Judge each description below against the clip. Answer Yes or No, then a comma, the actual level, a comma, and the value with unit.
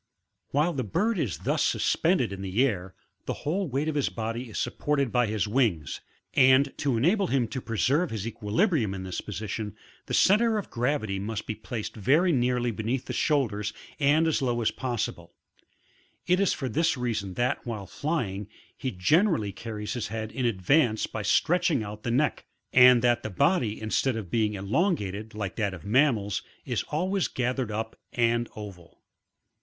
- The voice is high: No, low, 120 Hz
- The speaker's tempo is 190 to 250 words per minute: No, average, 175 wpm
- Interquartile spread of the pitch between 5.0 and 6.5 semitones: Yes, average, 5.3 semitones